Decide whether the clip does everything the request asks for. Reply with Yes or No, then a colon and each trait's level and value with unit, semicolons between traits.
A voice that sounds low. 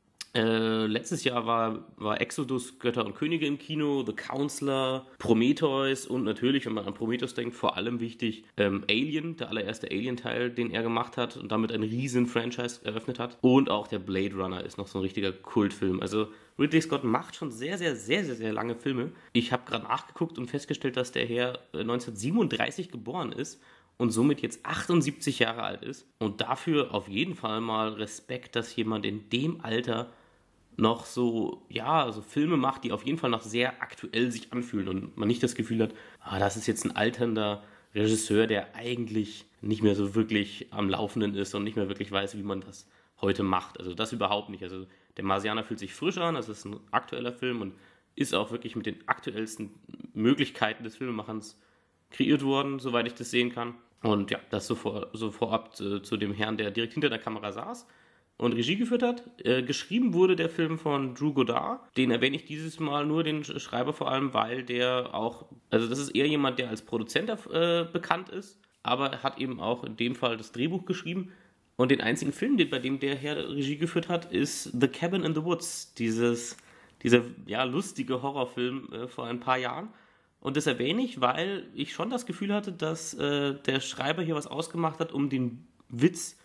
Yes: low, 120 Hz